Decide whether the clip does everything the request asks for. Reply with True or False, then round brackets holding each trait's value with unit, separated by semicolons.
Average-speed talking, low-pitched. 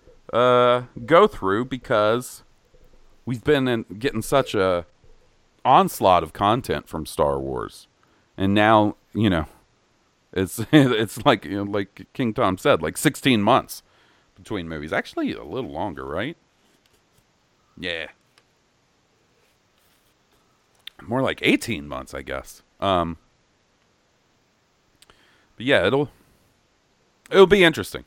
False (115 wpm; 110 Hz)